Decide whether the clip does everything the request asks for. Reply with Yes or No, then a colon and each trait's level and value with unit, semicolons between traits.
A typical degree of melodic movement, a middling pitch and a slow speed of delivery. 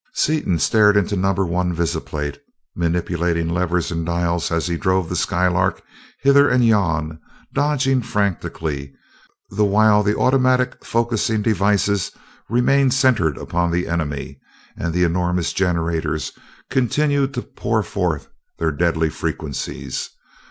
No: average, 5.0 semitones; very low, 90 Hz; slow, 125 wpm